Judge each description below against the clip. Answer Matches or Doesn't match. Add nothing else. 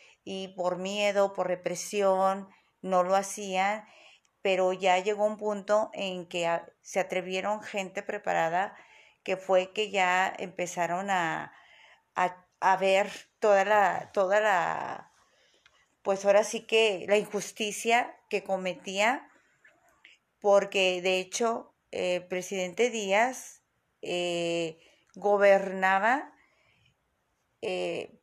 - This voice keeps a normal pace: Doesn't match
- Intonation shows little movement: Matches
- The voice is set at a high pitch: Matches